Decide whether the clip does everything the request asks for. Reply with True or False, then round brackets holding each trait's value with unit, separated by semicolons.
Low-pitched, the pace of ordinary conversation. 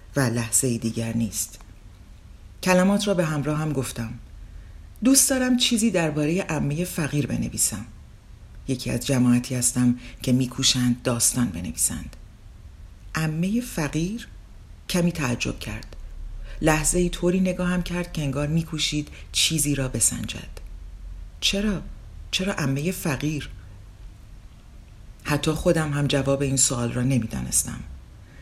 True (125 Hz; 115 wpm)